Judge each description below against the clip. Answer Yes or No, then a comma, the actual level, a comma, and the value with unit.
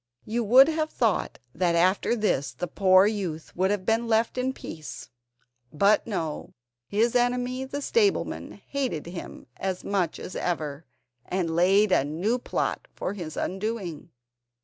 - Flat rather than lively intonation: No, wide, 5.5 semitones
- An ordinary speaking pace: Yes, average, 150 wpm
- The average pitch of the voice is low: No, high, 200 Hz